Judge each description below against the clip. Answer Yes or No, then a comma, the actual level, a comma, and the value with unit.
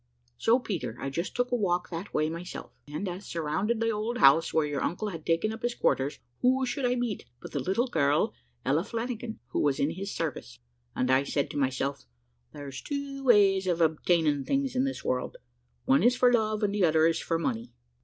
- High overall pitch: No, medium, 180 Hz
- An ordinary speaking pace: No, fast, 215 wpm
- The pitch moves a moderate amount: No, wide, 7.6 semitones